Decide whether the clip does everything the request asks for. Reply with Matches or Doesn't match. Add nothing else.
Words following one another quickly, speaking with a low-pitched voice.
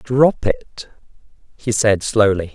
Doesn't match